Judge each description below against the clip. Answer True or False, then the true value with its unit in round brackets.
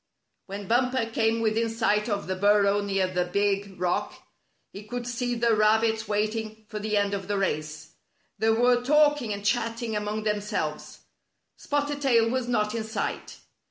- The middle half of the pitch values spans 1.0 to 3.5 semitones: True (2.4 semitones)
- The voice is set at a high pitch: True (215 Hz)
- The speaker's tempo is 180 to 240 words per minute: False (170 wpm)